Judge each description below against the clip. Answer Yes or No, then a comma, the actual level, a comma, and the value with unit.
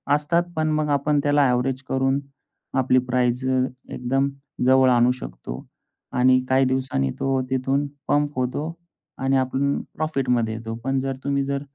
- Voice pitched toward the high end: No, low, 130 Hz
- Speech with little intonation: Yes, narrow, 1.8 semitones